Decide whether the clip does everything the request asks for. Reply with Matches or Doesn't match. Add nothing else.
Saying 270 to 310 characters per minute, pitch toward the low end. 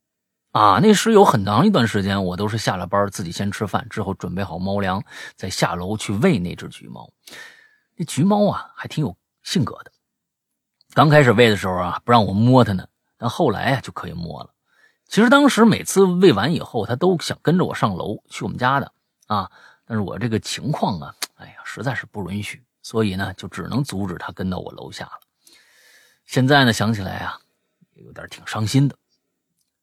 Matches